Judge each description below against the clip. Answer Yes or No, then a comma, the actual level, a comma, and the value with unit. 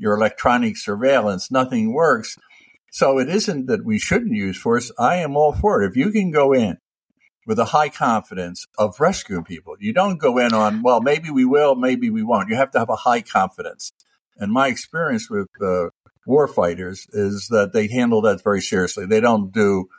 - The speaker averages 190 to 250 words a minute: Yes, average, 200 wpm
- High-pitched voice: No, low, 135 Hz